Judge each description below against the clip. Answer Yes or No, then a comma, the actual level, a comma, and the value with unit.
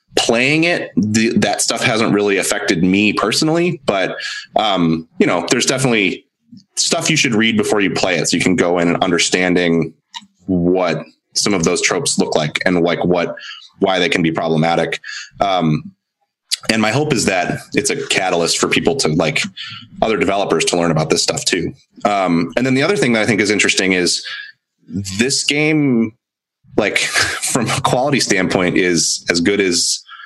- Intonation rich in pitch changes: Yes, wide, 8.5 semitones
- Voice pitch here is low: Yes, low, 110 Hz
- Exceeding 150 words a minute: Yes, average, 180 wpm